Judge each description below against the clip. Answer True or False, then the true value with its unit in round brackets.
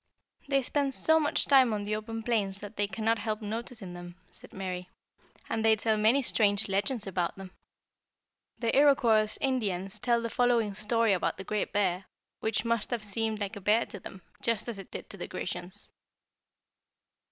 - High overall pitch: True (215 Hz)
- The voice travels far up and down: False (2.8 semitones)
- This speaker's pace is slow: False (180 wpm)